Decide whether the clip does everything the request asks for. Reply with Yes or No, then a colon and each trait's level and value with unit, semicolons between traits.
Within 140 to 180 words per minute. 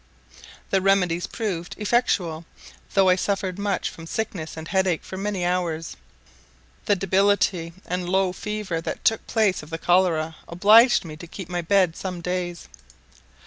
Yes: average, 150 wpm